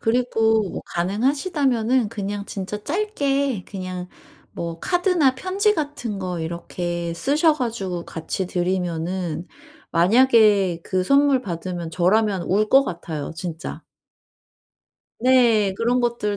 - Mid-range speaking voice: No, high, 205 Hz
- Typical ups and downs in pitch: No, wide, 6.5 semitones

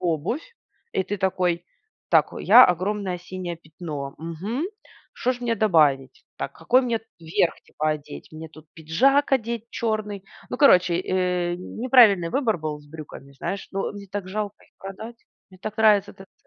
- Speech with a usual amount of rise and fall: Yes, average, 4.9 semitones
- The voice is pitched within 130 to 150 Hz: No, medium, 185 Hz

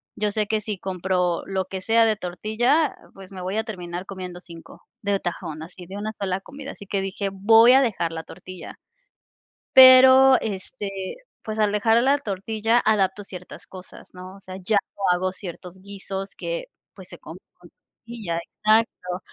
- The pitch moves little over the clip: No, average, 3.2 semitones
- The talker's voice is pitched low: No, high, 195 Hz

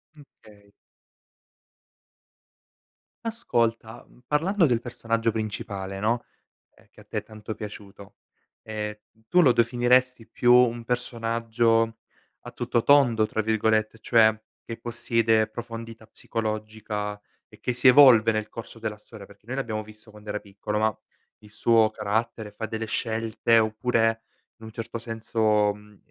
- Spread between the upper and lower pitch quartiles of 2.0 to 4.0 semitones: No, narrow, 1.5 semitones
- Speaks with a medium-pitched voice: No, low, 110 Hz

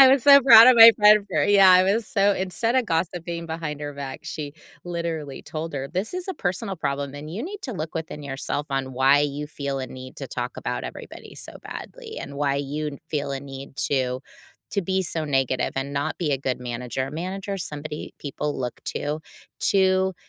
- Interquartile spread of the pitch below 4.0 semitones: No, wide, 5.4 semitones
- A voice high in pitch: No, medium, 155 Hz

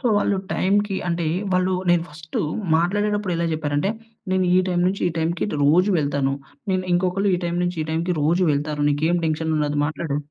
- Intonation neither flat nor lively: Yes, average, 3.3 semitones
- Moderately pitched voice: Yes, medium, 170 Hz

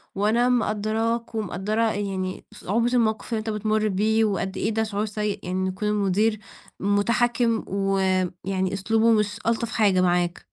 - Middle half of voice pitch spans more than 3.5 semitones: No, narrow, 2.4 semitones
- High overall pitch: Yes, high, 210 Hz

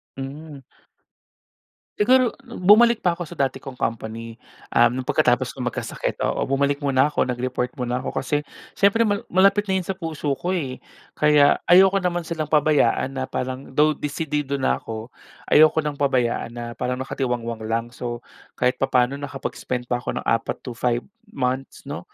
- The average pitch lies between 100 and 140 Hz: Yes, low, 135 Hz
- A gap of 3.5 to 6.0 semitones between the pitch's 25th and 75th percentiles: Yes, average, 4.2 semitones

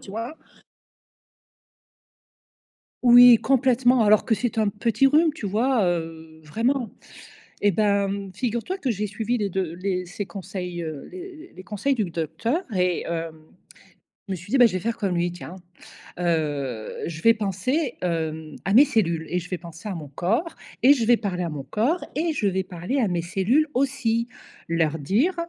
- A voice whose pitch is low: No, high, 200 Hz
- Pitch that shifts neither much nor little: No, wide, 6.0 semitones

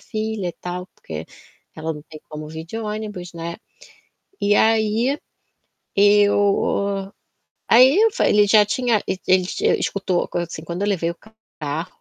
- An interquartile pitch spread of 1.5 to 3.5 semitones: No, average, 3.9 semitones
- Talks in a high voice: Yes, high, 195 Hz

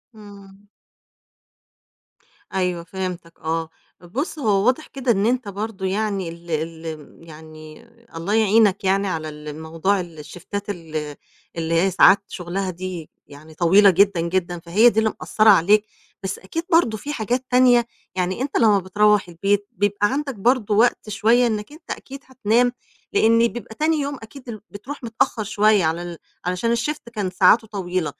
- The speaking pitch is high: Yes, high, 200 Hz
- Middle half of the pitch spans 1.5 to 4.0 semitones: No, average, 4.5 semitones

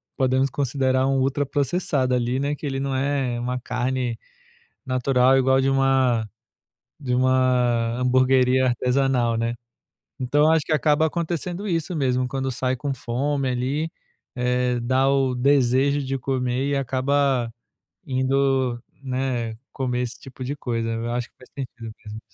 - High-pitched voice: No, low, 130 Hz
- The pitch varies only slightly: Yes, narrow, 1.7 semitones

